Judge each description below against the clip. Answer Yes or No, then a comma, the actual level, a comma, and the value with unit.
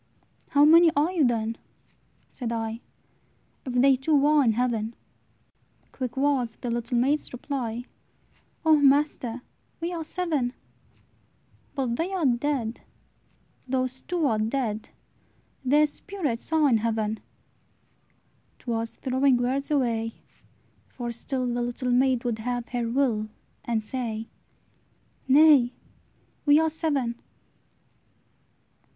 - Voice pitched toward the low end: No, very high, 255 Hz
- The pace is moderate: No, slow, 120 wpm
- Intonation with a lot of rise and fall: No, average, 3.6 semitones